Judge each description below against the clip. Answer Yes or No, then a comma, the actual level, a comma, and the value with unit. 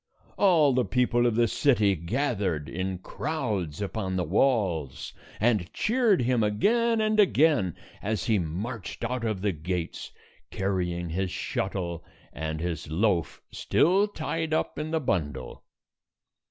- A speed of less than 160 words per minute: Yes, slow, 135 wpm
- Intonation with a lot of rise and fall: Yes, wide, 7.7 semitones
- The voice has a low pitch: Yes, low, 105 Hz